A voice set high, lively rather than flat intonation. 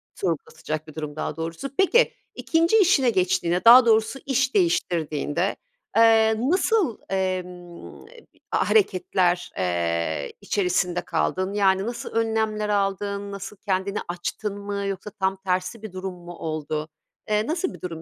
No: high, 195 Hz; average, 4.1 semitones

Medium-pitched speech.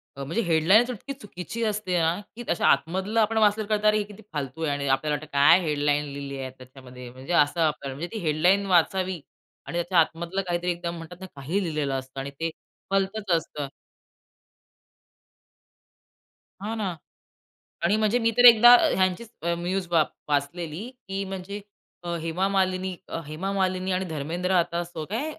Yes: medium, 175 Hz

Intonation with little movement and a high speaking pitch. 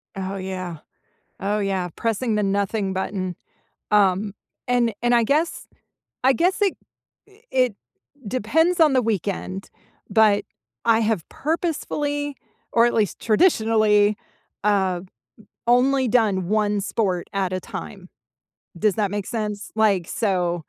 No: average, 3.8 semitones; high, 210 Hz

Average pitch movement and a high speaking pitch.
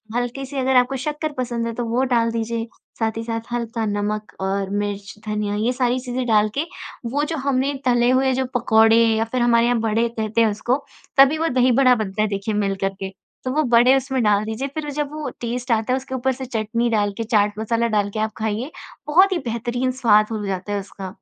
Yes: average, 3.2 semitones; high, 235 Hz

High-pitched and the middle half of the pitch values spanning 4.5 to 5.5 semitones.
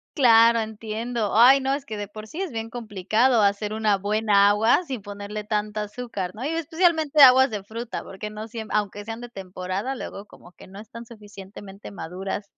No: high, 215 Hz; average, 2.9 semitones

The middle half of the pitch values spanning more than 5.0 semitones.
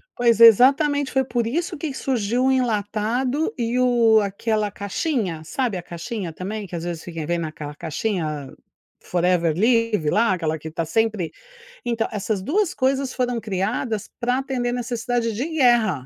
Yes: wide, 5.4 semitones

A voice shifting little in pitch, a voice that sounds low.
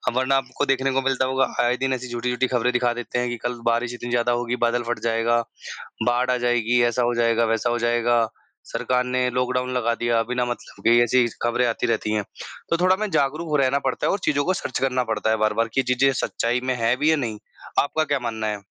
Yes: narrow, 1.6 semitones; low, 120 Hz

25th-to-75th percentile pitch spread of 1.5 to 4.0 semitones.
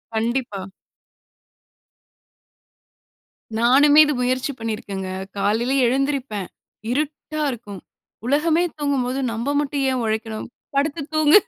No: average, 4.4 semitones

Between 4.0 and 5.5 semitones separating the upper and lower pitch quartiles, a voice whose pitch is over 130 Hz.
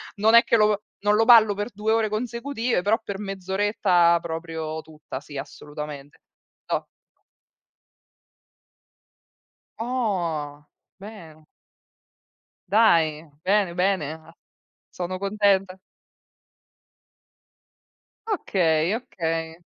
Yes: average, 4.8 semitones; high, 190 Hz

